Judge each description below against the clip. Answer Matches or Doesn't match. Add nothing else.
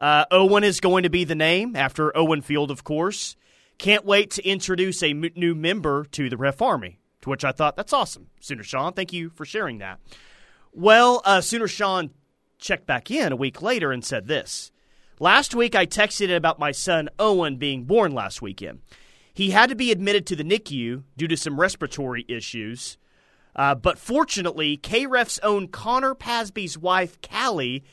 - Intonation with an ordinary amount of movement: Doesn't match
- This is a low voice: Doesn't match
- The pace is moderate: Matches